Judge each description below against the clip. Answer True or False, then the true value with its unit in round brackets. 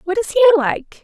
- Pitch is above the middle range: True (385 Hz)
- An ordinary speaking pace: False (230 wpm)